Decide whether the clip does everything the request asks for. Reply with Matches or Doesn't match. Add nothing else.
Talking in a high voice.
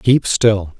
Doesn't match